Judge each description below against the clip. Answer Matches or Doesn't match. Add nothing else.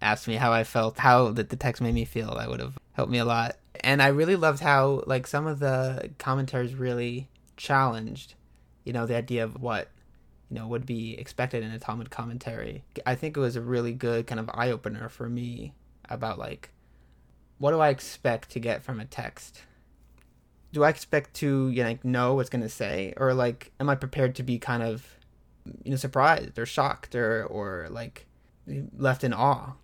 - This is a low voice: Matches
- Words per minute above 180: Matches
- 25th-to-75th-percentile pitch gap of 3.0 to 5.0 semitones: Doesn't match